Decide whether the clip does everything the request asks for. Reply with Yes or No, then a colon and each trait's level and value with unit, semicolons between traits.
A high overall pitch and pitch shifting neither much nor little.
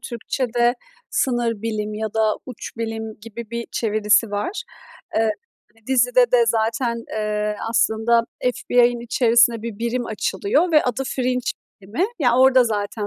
No: high, 230 Hz; narrow, 2.1 semitones